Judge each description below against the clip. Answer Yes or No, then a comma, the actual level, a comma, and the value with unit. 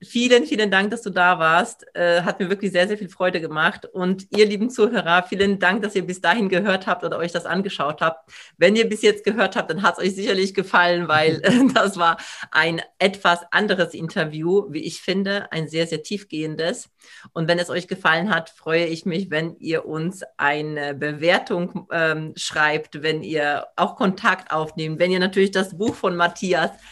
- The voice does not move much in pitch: No, average, 3.4 semitones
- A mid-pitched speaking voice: Yes, medium, 180 Hz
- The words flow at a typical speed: No, fast, 195 wpm